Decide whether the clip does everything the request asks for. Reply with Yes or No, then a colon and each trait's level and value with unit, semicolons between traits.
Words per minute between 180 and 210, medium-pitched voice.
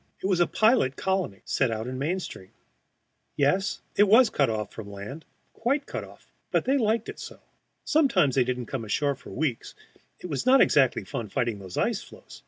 Yes: average, 190 wpm; medium, 145 Hz